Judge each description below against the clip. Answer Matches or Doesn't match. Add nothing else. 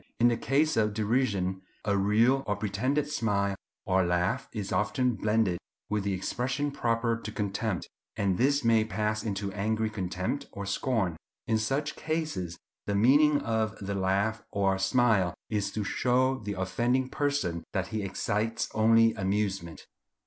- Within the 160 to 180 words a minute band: Doesn't match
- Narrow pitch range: Doesn't match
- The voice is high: Doesn't match